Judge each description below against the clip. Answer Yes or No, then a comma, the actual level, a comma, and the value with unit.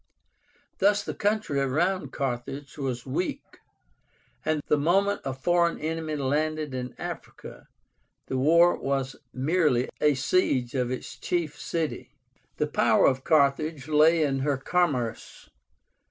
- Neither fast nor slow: No, slow, 125 wpm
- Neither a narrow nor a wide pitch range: Yes, average, 3.9 semitones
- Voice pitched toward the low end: No, medium, 150 Hz